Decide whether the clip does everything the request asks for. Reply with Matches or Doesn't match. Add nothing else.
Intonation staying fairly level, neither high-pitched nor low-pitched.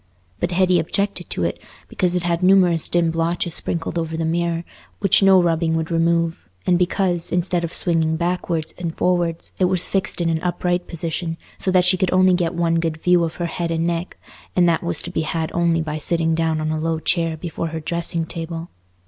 Matches